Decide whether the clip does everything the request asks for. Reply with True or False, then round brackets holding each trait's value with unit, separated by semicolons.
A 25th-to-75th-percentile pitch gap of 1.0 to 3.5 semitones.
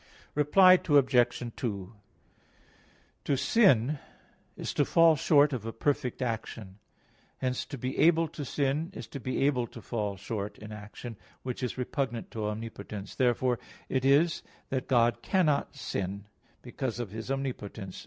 False (4.2 semitones)